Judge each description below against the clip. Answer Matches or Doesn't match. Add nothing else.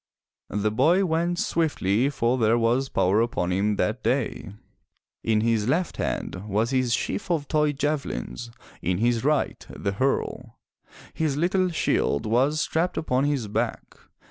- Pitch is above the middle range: Doesn't match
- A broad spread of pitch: Matches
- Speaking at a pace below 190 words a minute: Matches